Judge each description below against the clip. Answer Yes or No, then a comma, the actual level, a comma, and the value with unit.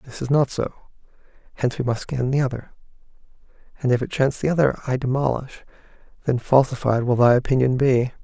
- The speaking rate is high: No, average, 175 wpm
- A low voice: Yes, low, 130 Hz